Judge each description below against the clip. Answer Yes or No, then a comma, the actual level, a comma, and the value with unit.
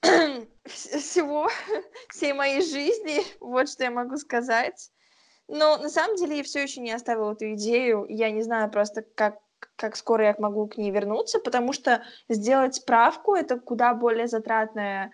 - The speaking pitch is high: Yes, high, 240 Hz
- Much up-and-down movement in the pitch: No, average, 4.6 semitones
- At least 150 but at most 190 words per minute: Yes, fast, 160 wpm